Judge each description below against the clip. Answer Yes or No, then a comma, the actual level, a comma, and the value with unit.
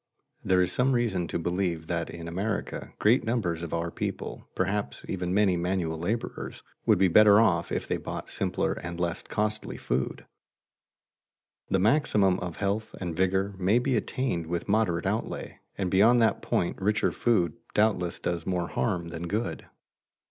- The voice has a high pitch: No, very low, 95 Hz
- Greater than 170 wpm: No, average, 165 wpm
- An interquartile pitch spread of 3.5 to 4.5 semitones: Yes, average, 3.9 semitones